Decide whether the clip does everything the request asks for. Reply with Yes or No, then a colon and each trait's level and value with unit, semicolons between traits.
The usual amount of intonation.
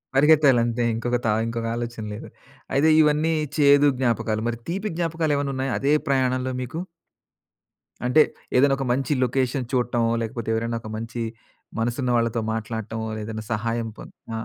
Yes: average, 3.4 semitones